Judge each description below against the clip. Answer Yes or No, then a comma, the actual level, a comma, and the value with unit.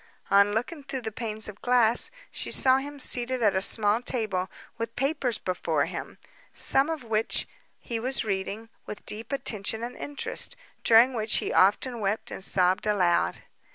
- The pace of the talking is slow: No, average, 165 wpm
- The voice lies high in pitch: Yes, high, 225 Hz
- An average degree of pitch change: Yes, average, 3.4 semitones